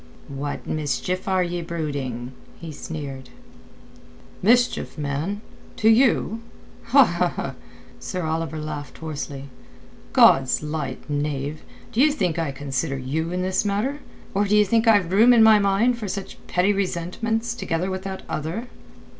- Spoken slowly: Yes, slow, 130 wpm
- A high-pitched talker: No, medium, 175 Hz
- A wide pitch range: Yes, wide, 5.7 semitones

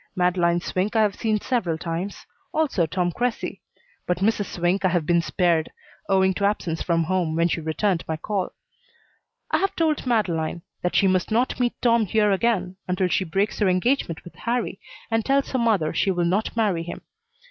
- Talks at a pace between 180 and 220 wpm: Yes, average, 190 wpm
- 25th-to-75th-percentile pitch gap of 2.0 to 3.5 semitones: No, average, 4.1 semitones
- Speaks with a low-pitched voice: No, high, 190 Hz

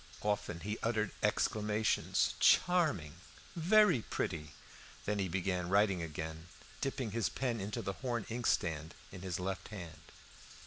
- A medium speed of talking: No, slow, 130 wpm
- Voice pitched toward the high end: No, low, 100 Hz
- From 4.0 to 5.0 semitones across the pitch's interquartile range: Yes, average, 4.6 semitones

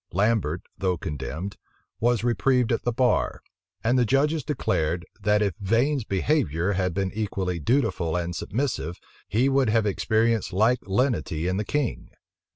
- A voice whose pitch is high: No, low, 105 Hz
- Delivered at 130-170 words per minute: Yes, average, 150 wpm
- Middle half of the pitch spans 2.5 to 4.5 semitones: No, average, 5.1 semitones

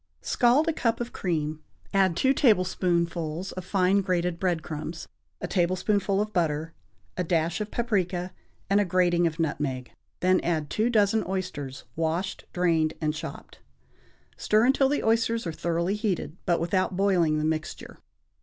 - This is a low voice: No, medium, 180 Hz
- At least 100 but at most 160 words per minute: Yes, average, 155 wpm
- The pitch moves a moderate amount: Yes, average, 3.6 semitones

